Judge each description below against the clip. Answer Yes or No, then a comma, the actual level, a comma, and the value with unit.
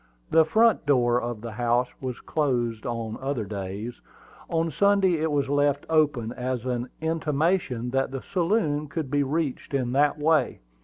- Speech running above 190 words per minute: No, average, 160 wpm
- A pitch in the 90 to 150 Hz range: Yes, low, 135 Hz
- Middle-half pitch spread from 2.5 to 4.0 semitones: No, average, 4.5 semitones